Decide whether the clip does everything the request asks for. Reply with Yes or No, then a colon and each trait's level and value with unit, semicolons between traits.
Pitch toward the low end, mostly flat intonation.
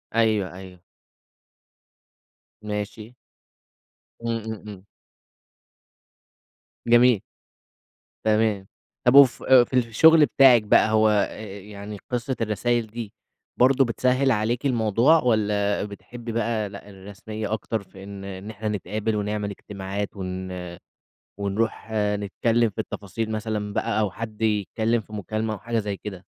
Yes: low, 110 Hz; narrow, 2.2 semitones